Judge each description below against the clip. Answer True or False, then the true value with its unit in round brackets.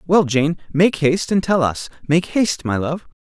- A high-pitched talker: False (160 Hz)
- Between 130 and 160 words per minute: False (205 wpm)